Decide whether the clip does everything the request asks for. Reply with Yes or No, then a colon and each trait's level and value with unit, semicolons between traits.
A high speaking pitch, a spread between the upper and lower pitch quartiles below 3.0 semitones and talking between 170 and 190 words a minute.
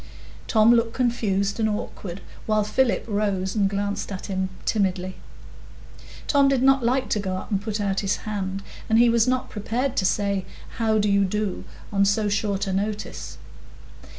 Yes: high, 210 Hz; narrow, 2.5 semitones; average, 175 wpm